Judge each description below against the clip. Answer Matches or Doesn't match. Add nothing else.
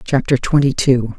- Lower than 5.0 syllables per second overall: Matches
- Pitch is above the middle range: Doesn't match